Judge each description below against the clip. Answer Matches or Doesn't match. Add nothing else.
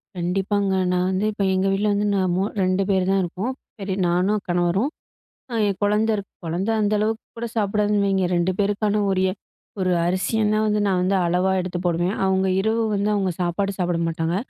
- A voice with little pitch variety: Matches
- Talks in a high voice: Matches